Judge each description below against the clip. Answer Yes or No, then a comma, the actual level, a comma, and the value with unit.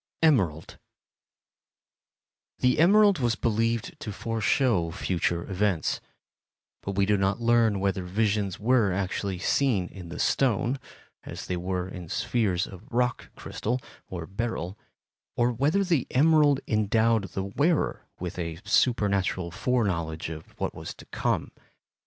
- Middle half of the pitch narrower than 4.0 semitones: No, average, 5.0 semitones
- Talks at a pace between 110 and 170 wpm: Yes, slow, 135 wpm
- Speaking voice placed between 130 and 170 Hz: No, low, 105 Hz